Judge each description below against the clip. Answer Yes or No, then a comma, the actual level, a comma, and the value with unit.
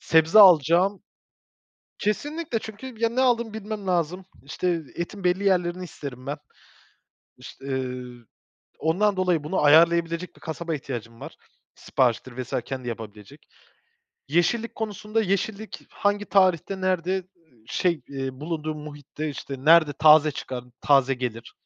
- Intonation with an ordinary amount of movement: No, wide, 5.8 semitones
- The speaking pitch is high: No, medium, 170 Hz